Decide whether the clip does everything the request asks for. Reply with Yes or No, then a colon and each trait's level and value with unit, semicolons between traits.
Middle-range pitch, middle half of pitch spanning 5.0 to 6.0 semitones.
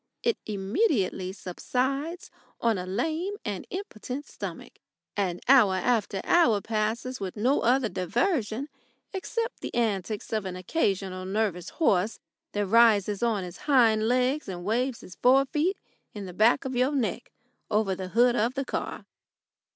No: high, 225 Hz; average, 5.3 semitones